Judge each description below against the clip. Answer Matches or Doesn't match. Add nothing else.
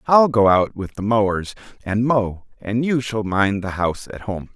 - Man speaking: Matches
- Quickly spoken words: Matches